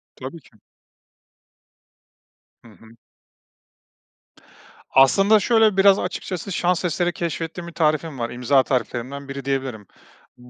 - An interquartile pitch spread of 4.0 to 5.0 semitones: No, wide, 5.5 semitones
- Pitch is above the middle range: No, medium, 155 Hz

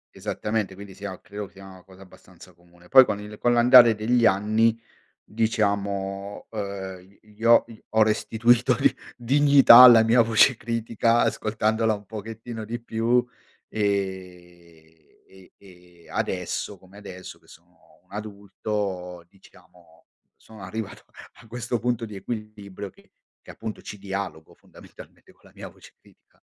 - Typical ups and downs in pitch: Yes, average, 3.1 semitones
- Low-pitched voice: Yes, low, 105 Hz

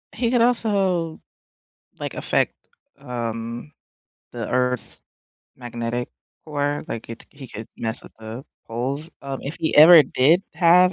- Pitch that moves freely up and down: Yes, wide, 6.0 semitones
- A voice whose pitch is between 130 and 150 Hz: Yes, medium, 140 Hz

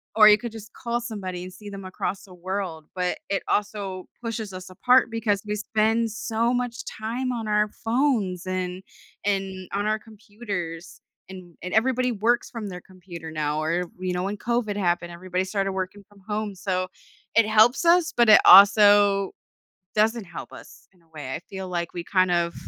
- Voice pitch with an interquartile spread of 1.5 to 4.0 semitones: Yes, average, 3.2 semitones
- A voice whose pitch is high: Yes, high, 200 Hz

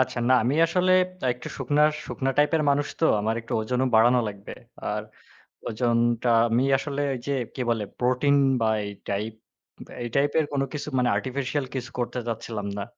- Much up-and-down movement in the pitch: No, average, 3.5 semitones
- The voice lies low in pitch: Yes, low, 125 Hz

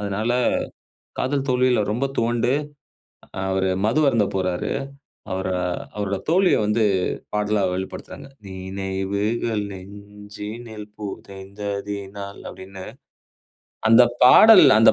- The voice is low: Yes, low, 105 Hz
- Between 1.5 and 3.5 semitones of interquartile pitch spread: Yes, average, 3.1 semitones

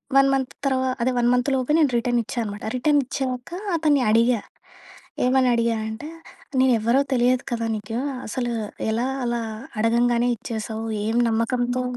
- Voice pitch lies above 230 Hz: Yes, high, 245 Hz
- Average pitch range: No, narrow, 2.1 semitones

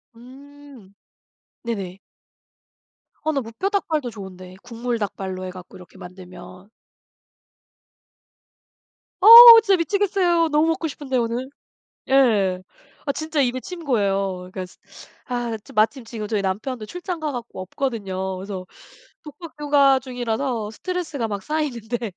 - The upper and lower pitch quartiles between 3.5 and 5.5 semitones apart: No, wide, 7.0 semitones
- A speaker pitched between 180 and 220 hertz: No, high, 240 Hz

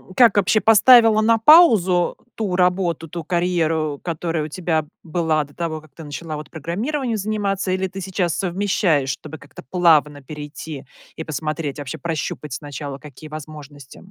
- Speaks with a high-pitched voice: No, medium, 165 Hz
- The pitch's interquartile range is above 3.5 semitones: Yes, average, 4.0 semitones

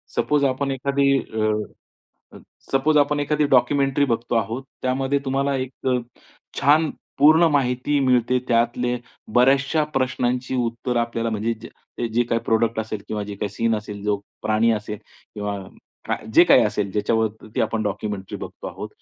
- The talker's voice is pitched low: Yes, low, 120 Hz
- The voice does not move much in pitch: No, average, 3.7 semitones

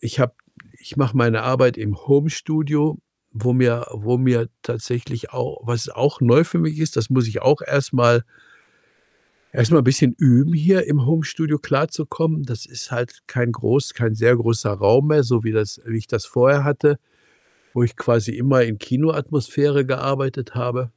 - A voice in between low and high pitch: No, low, 125 Hz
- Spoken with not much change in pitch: No, average, 3.4 semitones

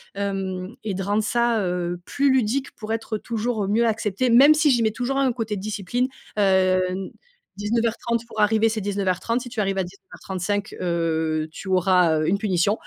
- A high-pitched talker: Yes, high, 210 Hz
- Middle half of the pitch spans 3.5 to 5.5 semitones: Yes, average, 3.8 semitones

